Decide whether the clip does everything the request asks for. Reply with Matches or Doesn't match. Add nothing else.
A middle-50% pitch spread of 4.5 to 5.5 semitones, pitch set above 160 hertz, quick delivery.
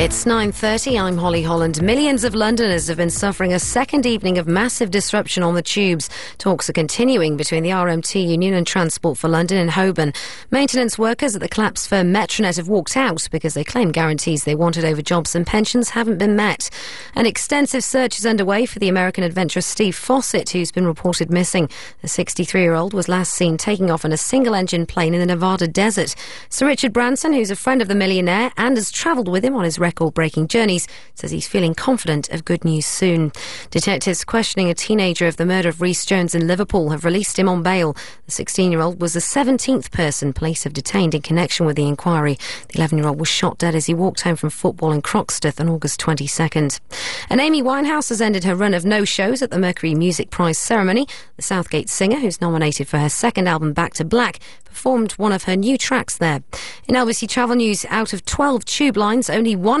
Matches